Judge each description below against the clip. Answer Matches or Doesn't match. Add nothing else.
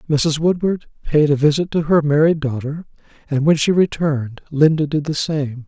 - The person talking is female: Doesn't match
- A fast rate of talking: Doesn't match